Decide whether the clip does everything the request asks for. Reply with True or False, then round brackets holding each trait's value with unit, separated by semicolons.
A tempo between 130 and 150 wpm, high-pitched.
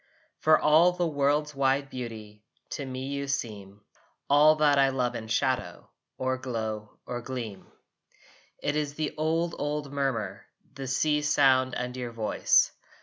False (145 wpm; 135 Hz)